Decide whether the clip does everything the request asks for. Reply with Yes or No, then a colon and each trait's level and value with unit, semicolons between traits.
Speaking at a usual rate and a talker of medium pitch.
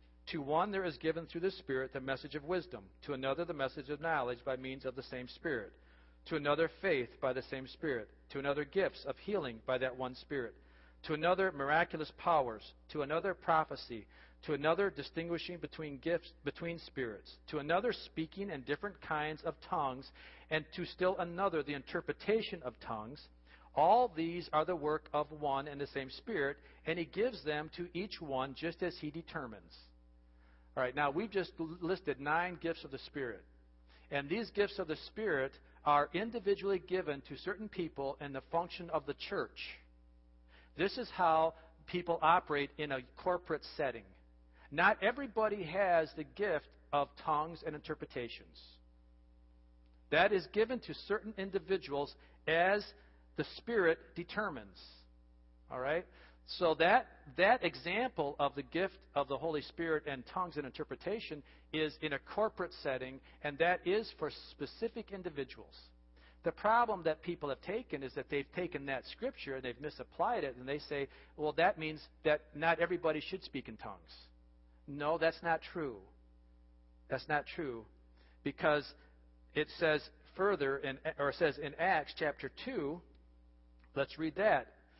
Yes: average, 160 wpm; medium, 150 Hz